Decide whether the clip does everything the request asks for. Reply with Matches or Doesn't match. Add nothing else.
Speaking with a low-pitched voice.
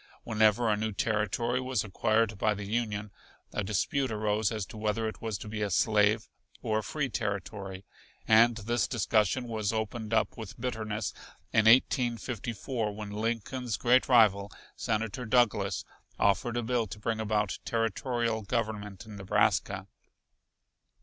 Matches